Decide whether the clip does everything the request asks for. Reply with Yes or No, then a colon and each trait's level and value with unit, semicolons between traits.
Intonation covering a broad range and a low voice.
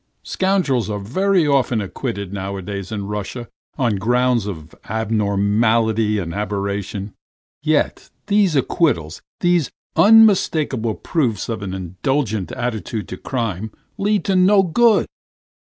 Yes: wide, 7.1 semitones; low, 110 Hz